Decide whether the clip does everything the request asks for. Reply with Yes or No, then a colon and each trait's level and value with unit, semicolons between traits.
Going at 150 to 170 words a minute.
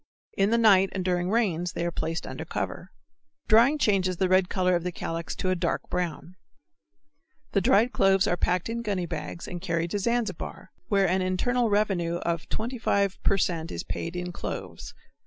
No: average, 185 wpm